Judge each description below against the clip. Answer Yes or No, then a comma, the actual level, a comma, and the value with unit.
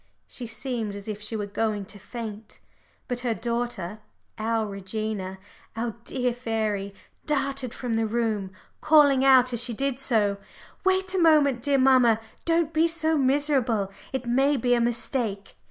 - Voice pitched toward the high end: Yes, high, 240 Hz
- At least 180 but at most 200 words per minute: No, average, 155 wpm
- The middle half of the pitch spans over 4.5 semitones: No, average, 3.9 semitones